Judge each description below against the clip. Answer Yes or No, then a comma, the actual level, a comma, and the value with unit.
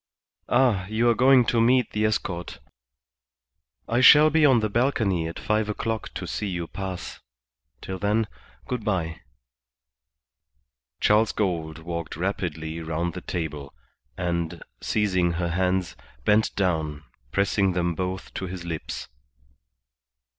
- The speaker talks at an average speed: No, slow, 130 wpm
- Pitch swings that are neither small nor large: Yes, average, 4.2 semitones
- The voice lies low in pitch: Yes, very low, 95 Hz